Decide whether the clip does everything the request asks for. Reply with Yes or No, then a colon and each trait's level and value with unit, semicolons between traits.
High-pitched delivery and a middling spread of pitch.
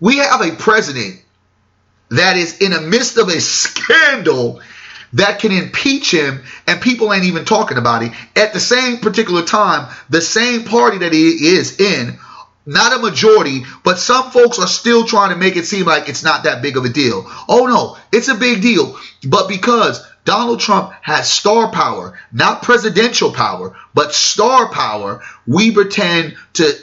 No: high, 205 Hz; wide, 6.6 semitones